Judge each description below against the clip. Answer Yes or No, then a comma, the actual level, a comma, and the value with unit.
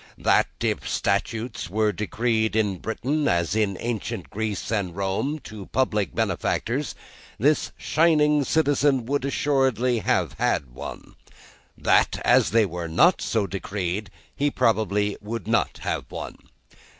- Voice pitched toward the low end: Yes, low, 110 Hz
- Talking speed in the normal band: No, slow, 130 wpm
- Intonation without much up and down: No, average, 5.1 semitones